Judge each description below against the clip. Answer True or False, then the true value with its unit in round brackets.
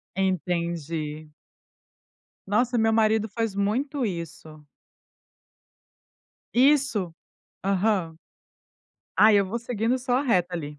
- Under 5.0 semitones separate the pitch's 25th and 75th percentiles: False (5.3 semitones)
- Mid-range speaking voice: False (200 Hz)